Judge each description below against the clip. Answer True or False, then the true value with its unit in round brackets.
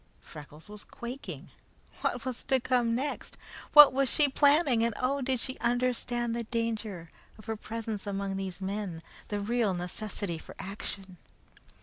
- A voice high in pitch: True (230 Hz)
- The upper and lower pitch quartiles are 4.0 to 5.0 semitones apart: True (4.3 semitones)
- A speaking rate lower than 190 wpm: True (150 wpm)